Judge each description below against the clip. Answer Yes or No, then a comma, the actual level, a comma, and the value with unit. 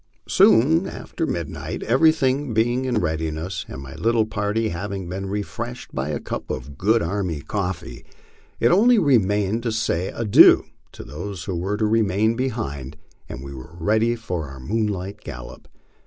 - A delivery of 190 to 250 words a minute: No, average, 160 wpm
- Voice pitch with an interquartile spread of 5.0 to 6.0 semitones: Yes, wide, 5.6 semitones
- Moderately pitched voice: No, low, 105 Hz